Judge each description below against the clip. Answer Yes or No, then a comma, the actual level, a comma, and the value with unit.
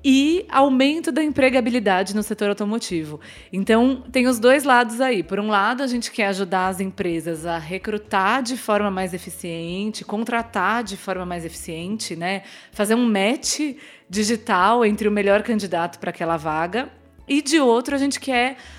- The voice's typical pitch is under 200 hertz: No, high, 215 Hz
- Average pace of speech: Yes, average, 165 wpm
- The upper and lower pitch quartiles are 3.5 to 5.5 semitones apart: Yes, average, 5.2 semitones